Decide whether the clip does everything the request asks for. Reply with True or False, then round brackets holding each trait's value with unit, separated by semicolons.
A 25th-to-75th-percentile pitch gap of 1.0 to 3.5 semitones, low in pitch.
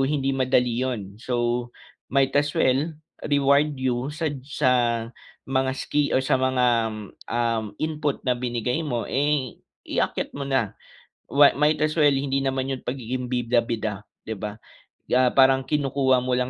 True (2.4 semitones; 130 Hz)